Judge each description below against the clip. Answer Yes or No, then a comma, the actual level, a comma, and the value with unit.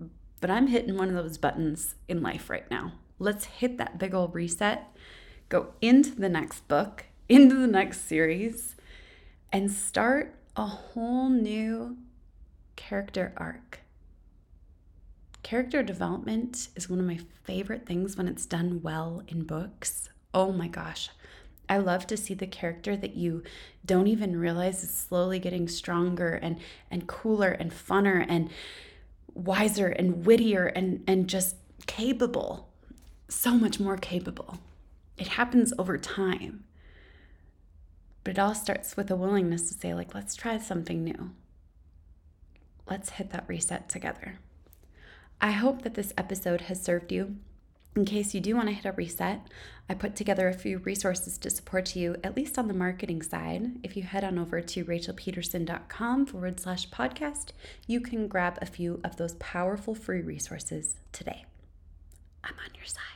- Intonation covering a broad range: No, average, 4.1 semitones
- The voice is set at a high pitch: No, medium, 180 Hz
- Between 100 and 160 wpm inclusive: Yes, average, 155 wpm